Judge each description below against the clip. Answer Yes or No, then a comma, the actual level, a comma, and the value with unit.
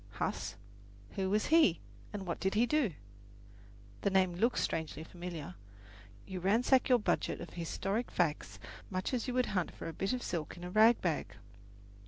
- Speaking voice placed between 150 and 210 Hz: Yes, high, 190 Hz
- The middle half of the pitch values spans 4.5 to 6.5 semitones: Yes, average, 5.2 semitones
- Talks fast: No, average, 175 wpm